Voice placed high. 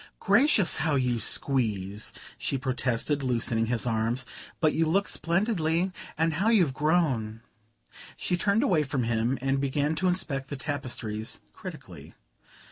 No: medium, 140 Hz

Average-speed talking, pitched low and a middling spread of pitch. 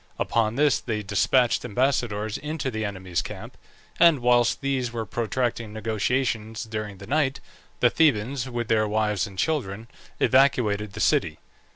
Yes: average, 145 wpm; low, 115 Hz; average, 3.5 semitones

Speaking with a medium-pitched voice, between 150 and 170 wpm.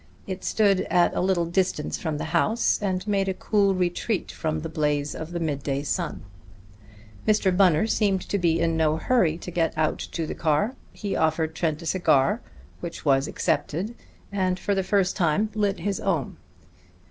No: medium, 175 Hz; average, 180 wpm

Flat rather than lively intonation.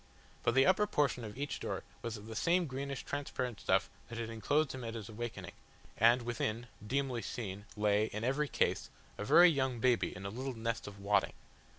No: average, 4.0 semitones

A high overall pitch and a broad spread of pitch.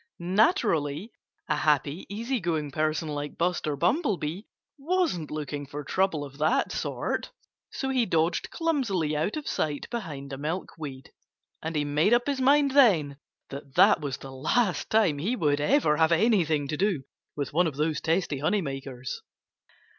No: medium, 160 Hz; wide, 6.4 semitones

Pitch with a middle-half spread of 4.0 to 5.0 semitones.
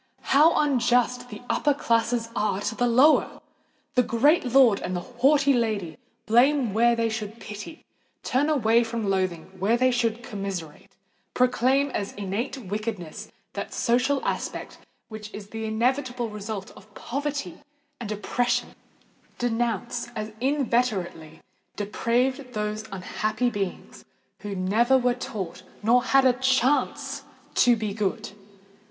No: average, 3.3 semitones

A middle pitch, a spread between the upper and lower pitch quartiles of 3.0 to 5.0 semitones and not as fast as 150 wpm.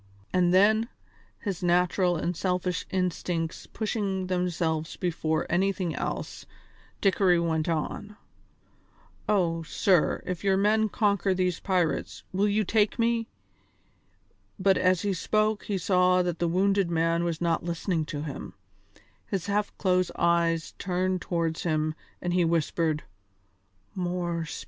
No: medium, 180 Hz; narrow, 2.6 semitones; slow, 135 wpm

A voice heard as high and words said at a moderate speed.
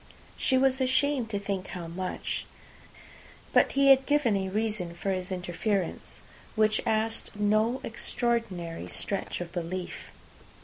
No: high, 210 Hz; slow, 130 wpm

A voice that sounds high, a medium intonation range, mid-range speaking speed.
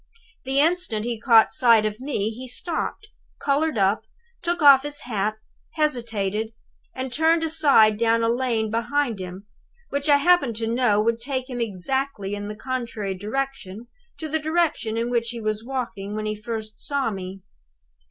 Yes: high, 235 Hz; average, 4.5 semitones; average, 165 wpm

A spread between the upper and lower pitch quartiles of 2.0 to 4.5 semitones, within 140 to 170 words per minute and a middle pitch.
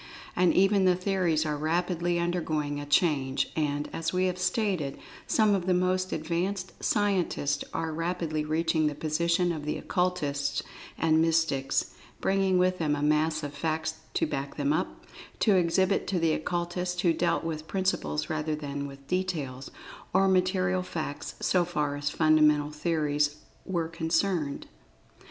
Yes: average, 3.3 semitones; average, 150 wpm; medium, 165 Hz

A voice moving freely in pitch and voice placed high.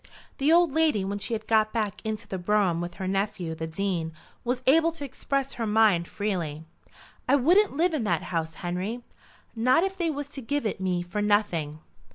Yes: wide, 7.4 semitones; high, 215 Hz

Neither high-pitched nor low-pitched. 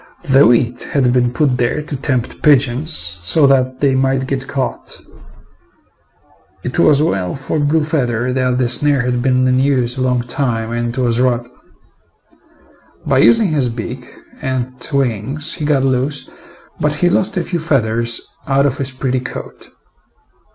No: low, 130 Hz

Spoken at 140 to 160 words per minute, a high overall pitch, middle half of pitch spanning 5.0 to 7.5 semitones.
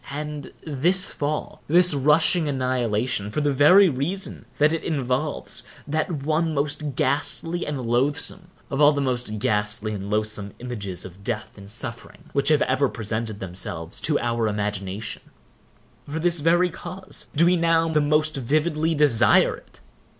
No: average, 145 wpm; medium, 140 Hz; wide, 5.6 semitones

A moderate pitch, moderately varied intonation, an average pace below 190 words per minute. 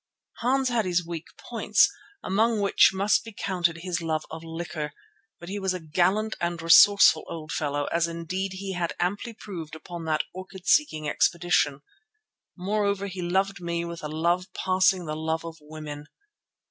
Yes: medium, 175 Hz; average, 3.1 semitones; average, 165 wpm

